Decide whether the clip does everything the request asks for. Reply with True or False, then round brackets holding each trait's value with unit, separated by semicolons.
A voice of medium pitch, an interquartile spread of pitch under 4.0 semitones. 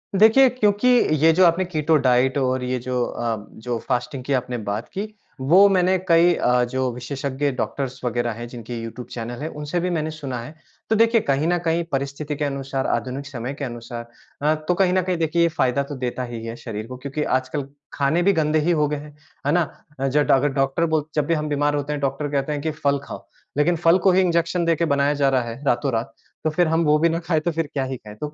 False (145 Hz; 4.5 semitones)